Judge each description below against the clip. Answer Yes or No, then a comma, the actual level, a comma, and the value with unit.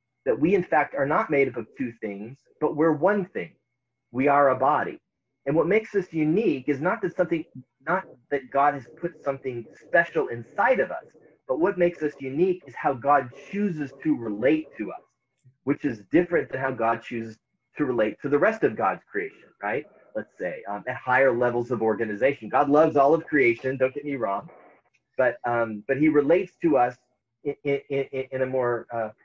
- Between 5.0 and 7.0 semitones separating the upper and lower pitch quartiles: No, average, 4.0 semitones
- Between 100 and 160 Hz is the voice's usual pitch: Yes, low, 135 Hz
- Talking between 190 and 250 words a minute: Yes, average, 200 wpm